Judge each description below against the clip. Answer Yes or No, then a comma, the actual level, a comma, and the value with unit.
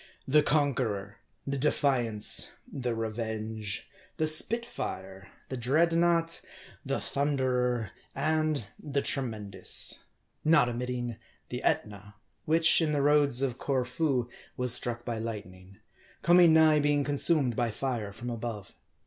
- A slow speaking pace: Yes, slow, 120 wpm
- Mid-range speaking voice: No, low, 125 Hz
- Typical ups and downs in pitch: Yes, average, 4.9 semitones